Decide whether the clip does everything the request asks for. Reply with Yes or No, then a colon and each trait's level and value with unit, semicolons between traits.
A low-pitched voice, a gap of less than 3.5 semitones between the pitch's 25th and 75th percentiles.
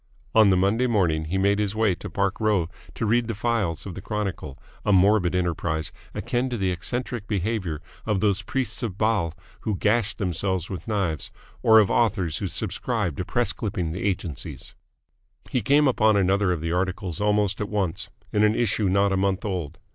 Yes: low, 100 Hz; average, 3.1 semitones